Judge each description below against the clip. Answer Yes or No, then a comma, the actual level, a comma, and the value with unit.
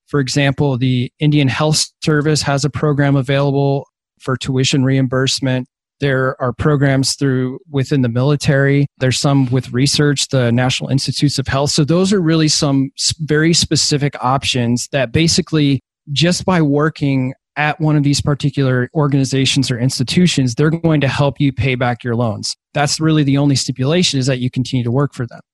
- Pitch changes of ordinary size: No, narrow, 2.2 semitones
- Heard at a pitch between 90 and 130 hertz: No, medium, 140 Hz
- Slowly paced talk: No, average, 170 wpm